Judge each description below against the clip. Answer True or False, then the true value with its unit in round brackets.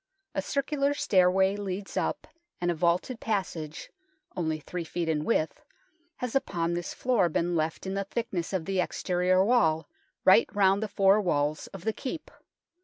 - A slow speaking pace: False (165 wpm)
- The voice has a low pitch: False (185 Hz)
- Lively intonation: False (3.3 semitones)